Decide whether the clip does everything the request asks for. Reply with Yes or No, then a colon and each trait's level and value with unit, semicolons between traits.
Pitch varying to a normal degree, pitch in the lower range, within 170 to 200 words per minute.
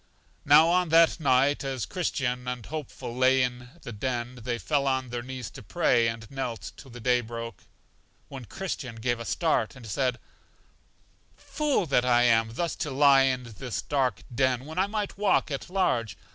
Yes: average, 3.3 semitones; low, 130 Hz; average, 180 wpm